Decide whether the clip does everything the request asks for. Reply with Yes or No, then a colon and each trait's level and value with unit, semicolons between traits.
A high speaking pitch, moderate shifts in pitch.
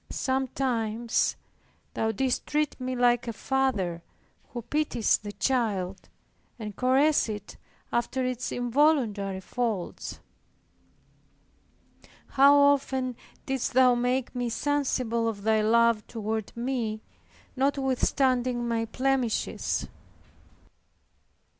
Yes: high, 245 Hz; average, 3.1 semitones